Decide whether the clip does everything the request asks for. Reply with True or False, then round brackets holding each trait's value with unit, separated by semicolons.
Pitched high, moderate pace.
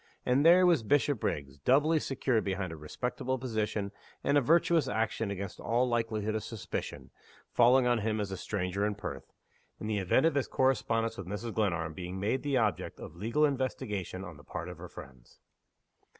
False (110 Hz; 180 wpm)